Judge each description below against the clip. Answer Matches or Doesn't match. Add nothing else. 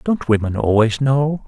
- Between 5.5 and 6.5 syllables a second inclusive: Doesn't match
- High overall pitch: Doesn't match